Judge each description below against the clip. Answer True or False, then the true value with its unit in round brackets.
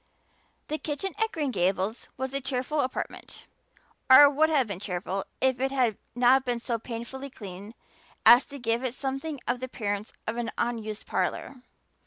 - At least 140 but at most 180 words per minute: True (170 wpm)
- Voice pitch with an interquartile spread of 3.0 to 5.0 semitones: True (3.4 semitones)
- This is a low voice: False (250 Hz)